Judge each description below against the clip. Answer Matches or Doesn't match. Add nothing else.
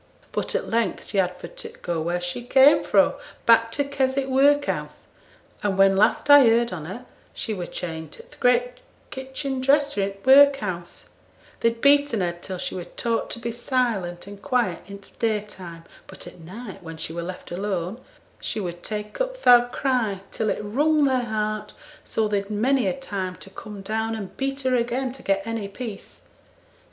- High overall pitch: Matches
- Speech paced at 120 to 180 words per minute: Doesn't match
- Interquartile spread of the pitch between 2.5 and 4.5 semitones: Doesn't match